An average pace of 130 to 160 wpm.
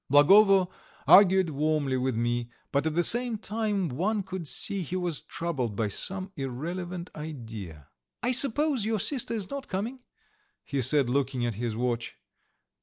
Yes: average, 155 wpm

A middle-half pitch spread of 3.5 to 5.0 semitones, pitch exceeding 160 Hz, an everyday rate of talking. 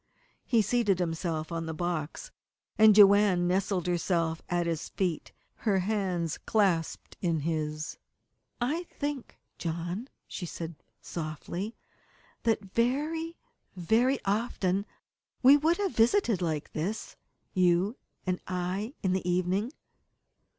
No: average, 4.7 semitones; medium, 185 Hz; slow, 115 wpm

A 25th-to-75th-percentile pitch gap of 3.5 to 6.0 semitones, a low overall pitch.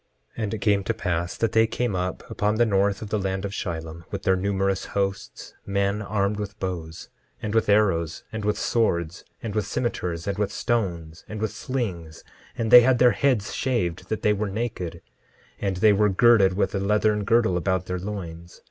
No: average, 2.9 semitones; low, 100 Hz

